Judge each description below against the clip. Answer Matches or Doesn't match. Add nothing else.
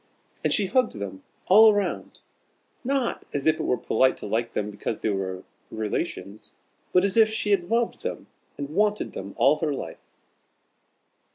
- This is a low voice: Doesn't match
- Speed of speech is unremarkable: Matches